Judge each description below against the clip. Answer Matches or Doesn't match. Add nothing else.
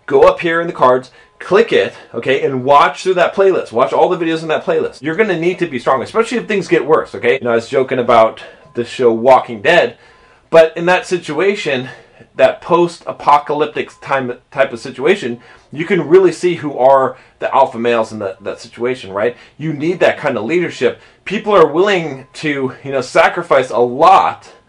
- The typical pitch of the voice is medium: Matches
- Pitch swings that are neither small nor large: Doesn't match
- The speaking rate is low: Doesn't match